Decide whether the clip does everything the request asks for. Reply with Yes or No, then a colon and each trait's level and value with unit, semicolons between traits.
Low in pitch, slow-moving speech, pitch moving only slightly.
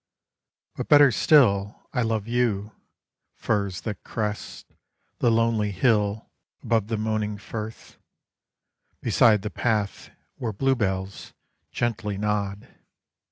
Yes: low, 105 Hz; slow, 105 wpm; narrow, 2.1 semitones